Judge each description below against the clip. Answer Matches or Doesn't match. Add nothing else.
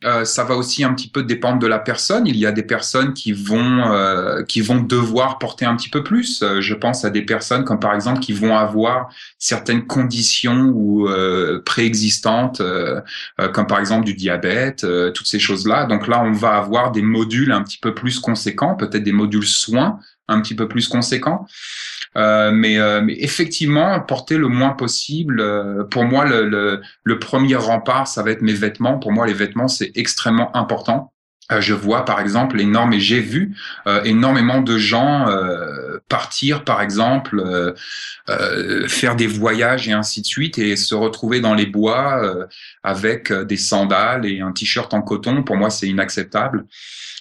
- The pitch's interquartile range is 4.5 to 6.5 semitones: Doesn't match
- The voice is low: Matches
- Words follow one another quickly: Doesn't match